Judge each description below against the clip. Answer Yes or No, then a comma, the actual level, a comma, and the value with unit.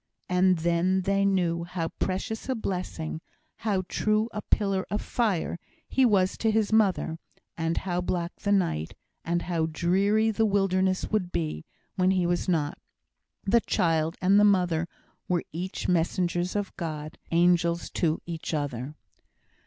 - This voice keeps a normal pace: Yes, average, 150 wpm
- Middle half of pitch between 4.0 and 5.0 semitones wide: No, average, 2.9 semitones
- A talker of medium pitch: Yes, medium, 180 Hz